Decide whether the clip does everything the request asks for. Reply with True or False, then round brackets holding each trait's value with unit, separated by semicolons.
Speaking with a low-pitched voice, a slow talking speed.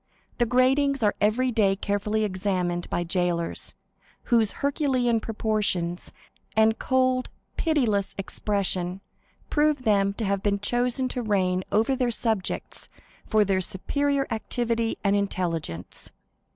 False (215 Hz; 120 wpm)